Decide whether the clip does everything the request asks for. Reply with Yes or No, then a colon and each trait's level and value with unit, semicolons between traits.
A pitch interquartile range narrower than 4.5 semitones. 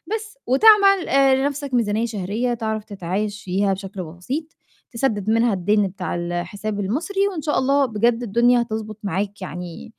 No: average, 5.1 semitones